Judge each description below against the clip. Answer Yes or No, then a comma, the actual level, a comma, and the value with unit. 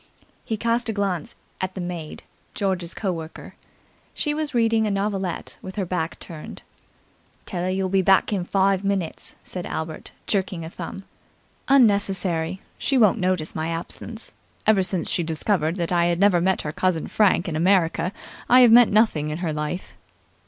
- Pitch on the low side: No, medium, 185 Hz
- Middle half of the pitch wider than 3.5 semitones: No, average, 3.2 semitones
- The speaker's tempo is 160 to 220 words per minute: Yes, average, 175 wpm